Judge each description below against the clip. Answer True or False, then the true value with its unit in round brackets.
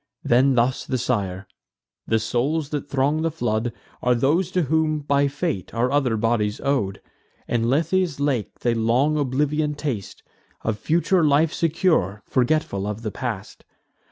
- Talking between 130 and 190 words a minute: True (150 wpm)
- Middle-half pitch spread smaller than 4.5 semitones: False (4.9 semitones)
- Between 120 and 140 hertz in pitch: True (135 Hz)